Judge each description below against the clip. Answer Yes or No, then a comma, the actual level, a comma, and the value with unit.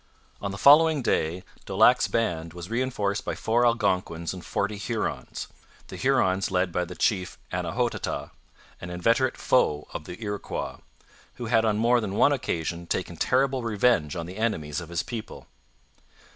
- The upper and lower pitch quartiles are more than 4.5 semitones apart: Yes, average, 5.1 semitones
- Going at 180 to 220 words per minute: No, average, 160 wpm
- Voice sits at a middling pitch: No, low, 105 Hz